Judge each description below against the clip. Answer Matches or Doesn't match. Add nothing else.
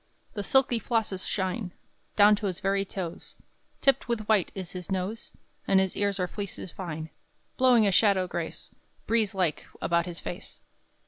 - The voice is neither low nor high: Doesn't match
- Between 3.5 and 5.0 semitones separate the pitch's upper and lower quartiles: Doesn't match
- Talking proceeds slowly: Doesn't match